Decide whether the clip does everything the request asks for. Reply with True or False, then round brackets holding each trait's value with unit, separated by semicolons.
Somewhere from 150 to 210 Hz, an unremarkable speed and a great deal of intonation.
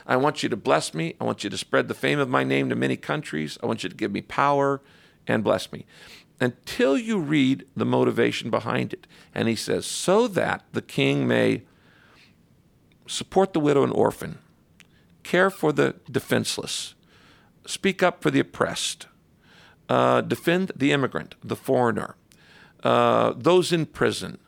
False (140 Hz; 165 wpm; 7.6 semitones)